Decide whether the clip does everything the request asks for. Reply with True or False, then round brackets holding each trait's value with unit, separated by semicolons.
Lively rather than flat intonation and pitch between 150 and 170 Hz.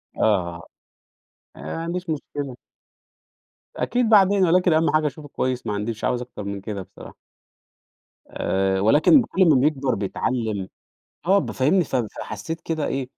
False (7.7 semitones; 135 Hz)